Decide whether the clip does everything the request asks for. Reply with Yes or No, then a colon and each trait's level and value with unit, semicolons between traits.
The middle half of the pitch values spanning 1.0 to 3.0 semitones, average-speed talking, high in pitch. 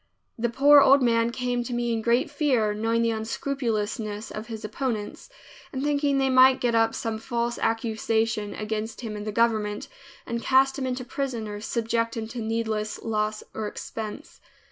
Yes: narrow, 2.5 semitones; average, 175 wpm; high, 230 Hz